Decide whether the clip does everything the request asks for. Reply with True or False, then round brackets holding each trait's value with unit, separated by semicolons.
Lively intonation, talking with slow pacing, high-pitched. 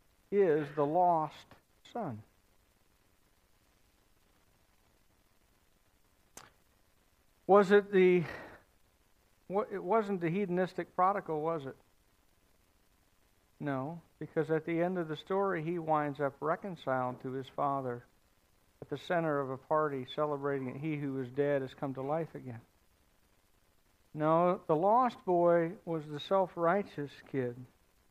False (8.7 semitones; 120 wpm; 145 Hz)